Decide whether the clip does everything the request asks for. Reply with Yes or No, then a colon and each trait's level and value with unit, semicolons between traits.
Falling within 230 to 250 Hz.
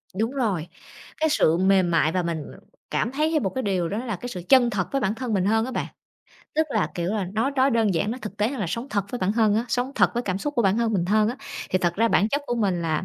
No: high, 215 Hz